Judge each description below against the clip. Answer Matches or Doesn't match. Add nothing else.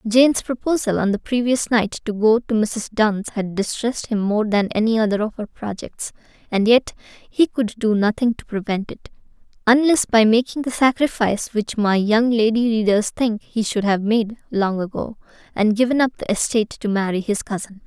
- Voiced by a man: Doesn't match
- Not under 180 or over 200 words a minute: Matches